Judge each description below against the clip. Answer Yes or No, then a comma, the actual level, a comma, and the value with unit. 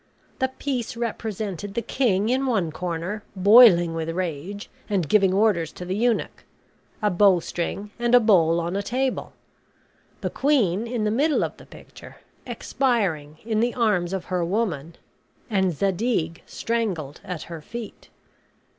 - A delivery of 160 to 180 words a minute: No, average, 145 wpm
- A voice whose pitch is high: Yes, high, 200 Hz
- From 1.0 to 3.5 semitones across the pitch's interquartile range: No, average, 5.1 semitones